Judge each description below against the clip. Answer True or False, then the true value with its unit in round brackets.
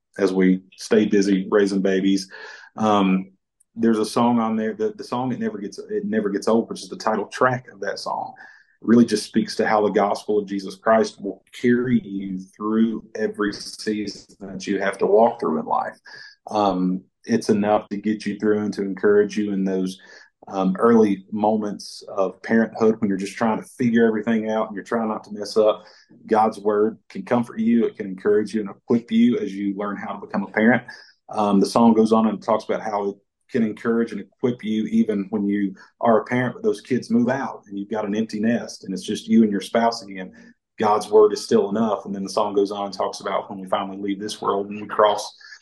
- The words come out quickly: True (225 wpm)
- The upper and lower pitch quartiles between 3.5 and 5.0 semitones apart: False (2.4 semitones)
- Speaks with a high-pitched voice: False (105 Hz)